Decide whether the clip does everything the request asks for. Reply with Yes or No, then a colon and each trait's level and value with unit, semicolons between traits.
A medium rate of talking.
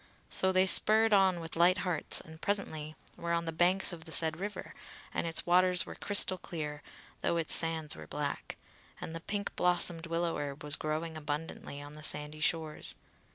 Yes: average, 185 wpm